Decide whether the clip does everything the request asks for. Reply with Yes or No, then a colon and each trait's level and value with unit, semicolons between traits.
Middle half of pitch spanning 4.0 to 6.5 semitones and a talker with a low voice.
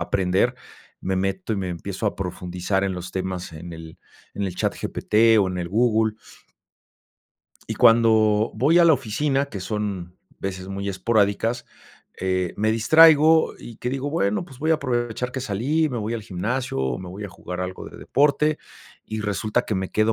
Yes: average, 4.6 semitones; low, 105 Hz